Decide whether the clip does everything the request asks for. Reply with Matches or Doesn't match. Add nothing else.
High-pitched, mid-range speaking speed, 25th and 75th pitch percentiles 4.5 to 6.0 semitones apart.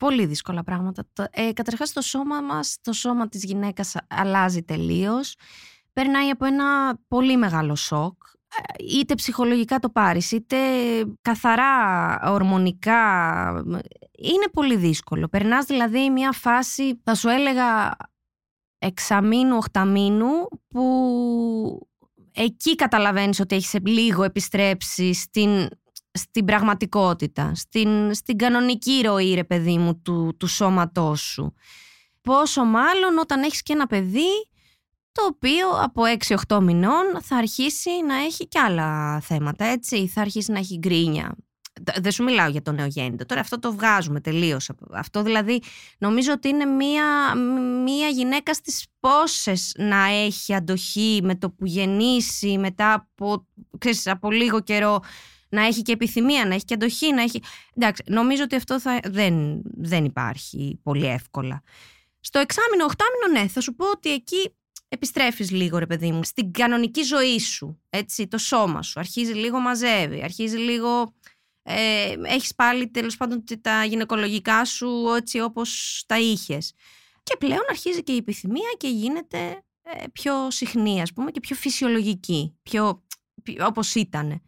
Matches